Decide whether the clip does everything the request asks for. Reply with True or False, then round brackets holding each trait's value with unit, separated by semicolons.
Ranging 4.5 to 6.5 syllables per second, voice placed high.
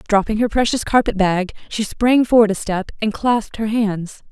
True (5.0 syllables/s; 215 Hz)